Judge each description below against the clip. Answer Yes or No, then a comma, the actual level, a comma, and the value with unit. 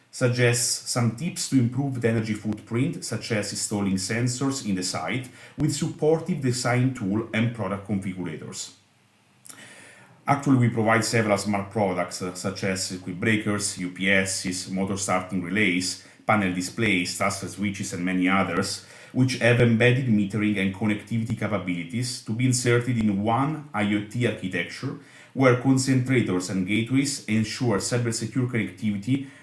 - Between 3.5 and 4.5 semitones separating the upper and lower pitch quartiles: Yes, average, 4.2 semitones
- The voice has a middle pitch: No, low, 110 Hz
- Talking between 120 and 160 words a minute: Yes, slow, 135 wpm